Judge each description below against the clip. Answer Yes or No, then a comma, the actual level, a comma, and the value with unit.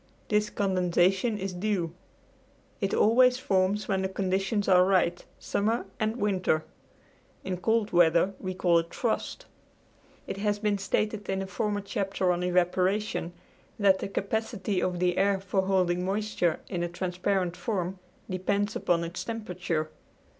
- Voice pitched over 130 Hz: Yes, high, 190 Hz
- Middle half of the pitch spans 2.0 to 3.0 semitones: Yes, narrow, 2.4 semitones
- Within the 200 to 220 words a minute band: No, average, 145 wpm